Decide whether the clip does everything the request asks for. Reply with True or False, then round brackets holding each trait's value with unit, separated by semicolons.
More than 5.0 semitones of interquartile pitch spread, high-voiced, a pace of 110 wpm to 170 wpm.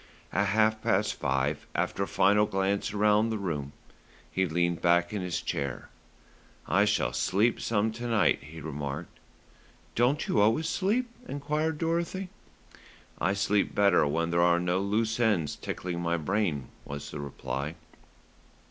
False (5.4 semitones; 95 Hz; 150 wpm)